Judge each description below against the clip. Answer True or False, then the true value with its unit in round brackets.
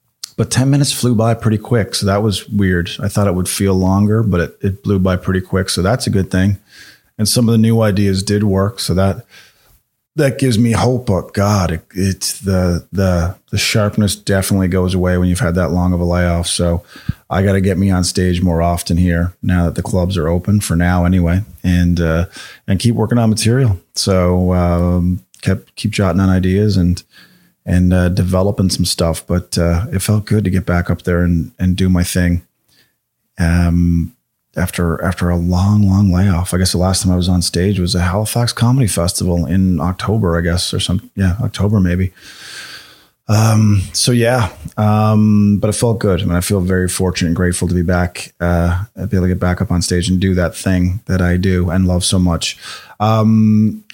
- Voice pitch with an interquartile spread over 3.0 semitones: False (2.7 semitones)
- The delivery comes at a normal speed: False (210 wpm)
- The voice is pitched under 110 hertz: True (95 Hz)